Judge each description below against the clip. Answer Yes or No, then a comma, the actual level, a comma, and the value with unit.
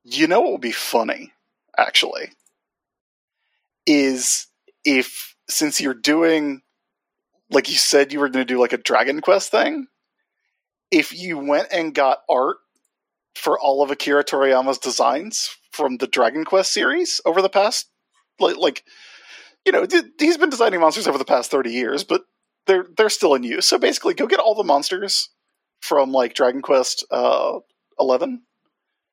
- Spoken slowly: No, average, 155 wpm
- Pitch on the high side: Yes, high, 195 Hz